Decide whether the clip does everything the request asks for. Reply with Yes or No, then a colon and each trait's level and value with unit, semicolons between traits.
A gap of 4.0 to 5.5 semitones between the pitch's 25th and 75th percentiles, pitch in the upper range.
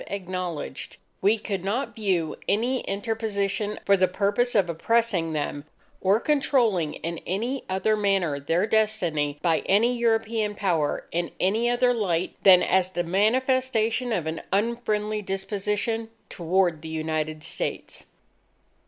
Yes: average, 4.4 semitones; high, 200 Hz